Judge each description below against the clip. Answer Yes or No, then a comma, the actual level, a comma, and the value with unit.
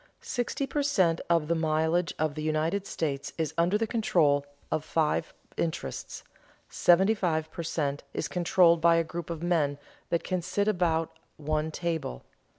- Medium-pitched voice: Yes, medium, 165 Hz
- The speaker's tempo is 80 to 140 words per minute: No, average, 160 wpm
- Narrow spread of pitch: Yes, narrow, 2.3 semitones